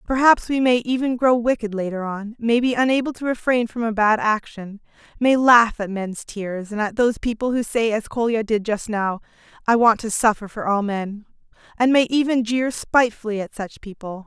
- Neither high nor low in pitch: No, high, 225 Hz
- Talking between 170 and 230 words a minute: Yes, average, 200 wpm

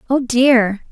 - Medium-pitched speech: No, high, 245 Hz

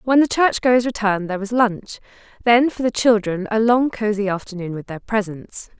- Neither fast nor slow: Yes, average, 185 wpm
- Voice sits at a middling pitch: No, high, 215 Hz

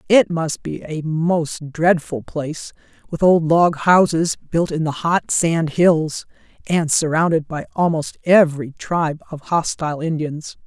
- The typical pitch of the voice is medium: Yes, medium, 160 Hz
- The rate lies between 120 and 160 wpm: Yes, average, 140 wpm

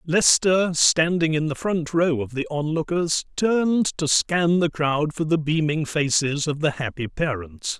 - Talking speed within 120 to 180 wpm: Yes, average, 170 wpm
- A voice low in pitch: No, medium, 155 Hz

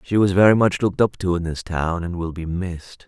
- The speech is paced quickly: Yes, fast, 275 wpm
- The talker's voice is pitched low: Yes, very low, 90 Hz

